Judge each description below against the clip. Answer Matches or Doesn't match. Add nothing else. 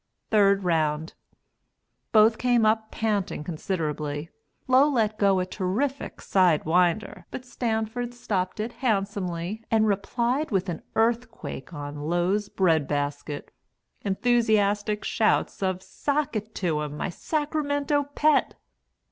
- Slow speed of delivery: Matches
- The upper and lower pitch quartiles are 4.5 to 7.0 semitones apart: Matches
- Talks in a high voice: Matches